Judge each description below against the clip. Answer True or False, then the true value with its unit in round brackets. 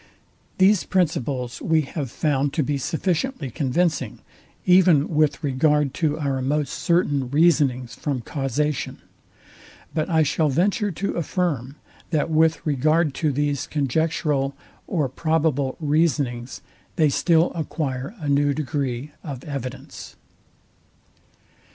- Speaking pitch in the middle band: True (150 Hz)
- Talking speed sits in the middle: False (115 wpm)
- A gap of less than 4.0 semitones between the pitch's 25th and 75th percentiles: True (3.0 semitones)